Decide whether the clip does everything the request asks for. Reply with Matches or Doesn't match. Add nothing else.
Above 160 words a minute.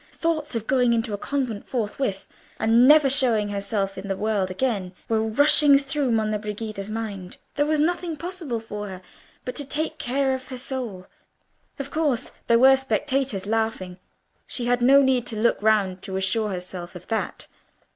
Matches